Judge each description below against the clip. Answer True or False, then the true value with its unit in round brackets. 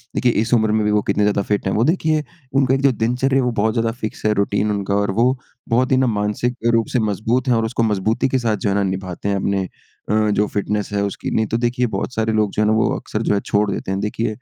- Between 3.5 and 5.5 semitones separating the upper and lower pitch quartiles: False (2.9 semitones)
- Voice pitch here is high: False (110 Hz)